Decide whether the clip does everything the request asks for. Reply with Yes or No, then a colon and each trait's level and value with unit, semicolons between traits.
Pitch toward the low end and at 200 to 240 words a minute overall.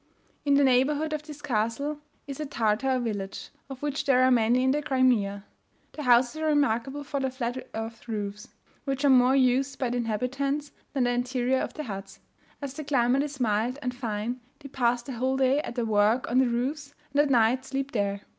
No: very high, 255 Hz; fast, 205 wpm